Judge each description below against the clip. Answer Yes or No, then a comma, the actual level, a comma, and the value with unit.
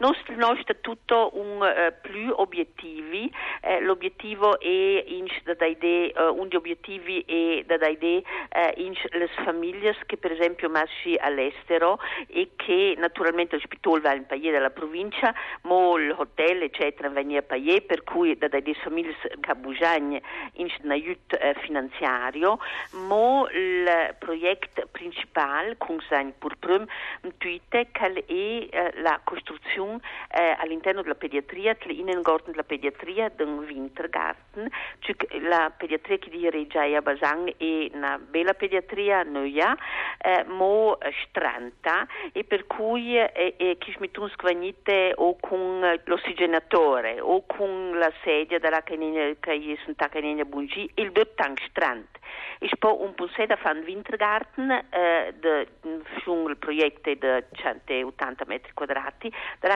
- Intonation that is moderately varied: No, wide, 5.8 semitones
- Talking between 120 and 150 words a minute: Yes, average, 140 wpm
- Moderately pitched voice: Yes, medium, 175 Hz